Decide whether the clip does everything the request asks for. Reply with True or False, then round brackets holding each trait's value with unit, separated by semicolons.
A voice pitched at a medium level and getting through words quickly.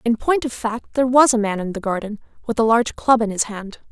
False (230 Hz; 275 wpm)